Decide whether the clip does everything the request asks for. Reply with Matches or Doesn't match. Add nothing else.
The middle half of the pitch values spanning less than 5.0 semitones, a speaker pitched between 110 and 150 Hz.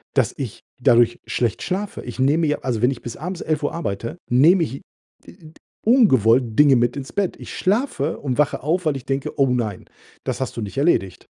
Doesn't match